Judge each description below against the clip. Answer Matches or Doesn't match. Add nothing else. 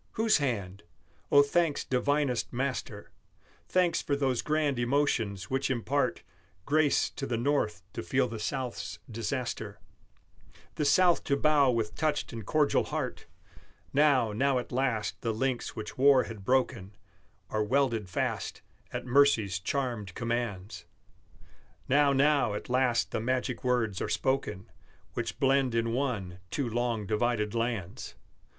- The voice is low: Matches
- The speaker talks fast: Doesn't match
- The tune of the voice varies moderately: Matches